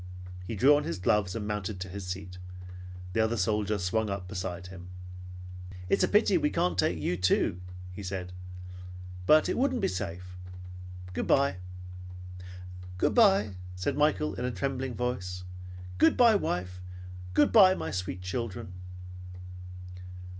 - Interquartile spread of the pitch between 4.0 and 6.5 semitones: Yes, wide, 5.6 semitones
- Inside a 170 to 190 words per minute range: No, average, 145 wpm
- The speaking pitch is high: No, low, 100 Hz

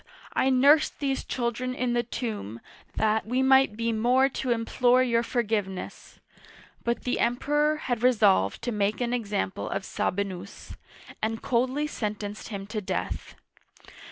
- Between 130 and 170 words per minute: Yes, average, 145 wpm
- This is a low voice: No, high, 235 Hz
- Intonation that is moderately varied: Yes, average, 3.2 semitones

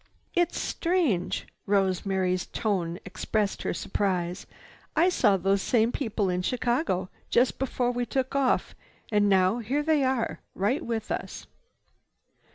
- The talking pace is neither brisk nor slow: No, slow, 130 wpm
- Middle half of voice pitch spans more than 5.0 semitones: Yes, wide, 5.4 semitones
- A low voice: No, high, 215 Hz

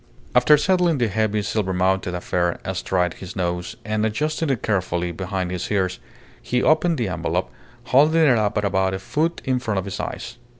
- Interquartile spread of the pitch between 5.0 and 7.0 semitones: Yes, wide, 5.4 semitones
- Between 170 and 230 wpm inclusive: Yes, average, 180 wpm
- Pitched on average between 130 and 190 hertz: No, low, 105 Hz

